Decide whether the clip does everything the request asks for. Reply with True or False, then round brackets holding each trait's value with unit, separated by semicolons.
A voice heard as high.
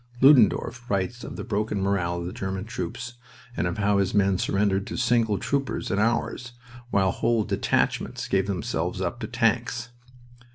False (100 Hz)